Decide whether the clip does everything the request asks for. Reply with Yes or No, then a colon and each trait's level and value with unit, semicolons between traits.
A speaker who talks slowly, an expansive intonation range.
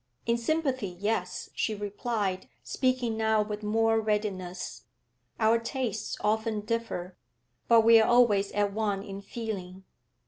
No: slow, 130 wpm; narrow, 2.5 semitones